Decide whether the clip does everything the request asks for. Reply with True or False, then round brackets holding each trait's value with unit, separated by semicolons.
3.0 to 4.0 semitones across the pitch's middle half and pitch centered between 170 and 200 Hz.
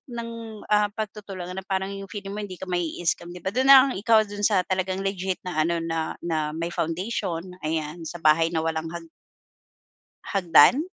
True (3.6 semitones; 185 Hz)